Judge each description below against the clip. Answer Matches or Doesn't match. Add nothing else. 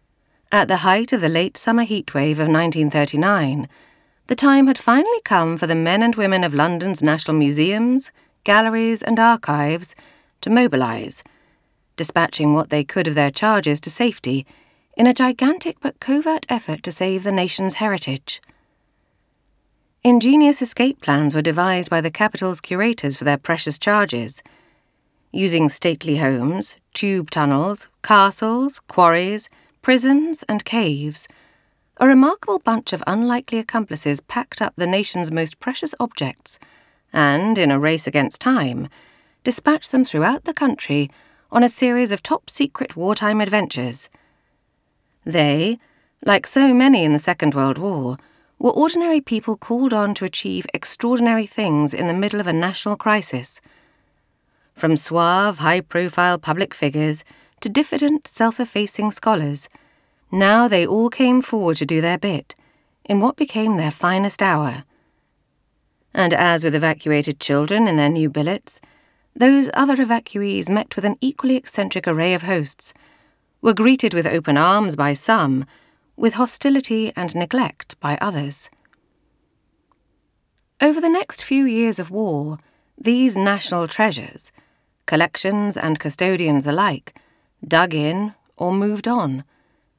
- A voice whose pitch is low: Doesn't match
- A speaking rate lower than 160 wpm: Matches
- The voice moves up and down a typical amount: Doesn't match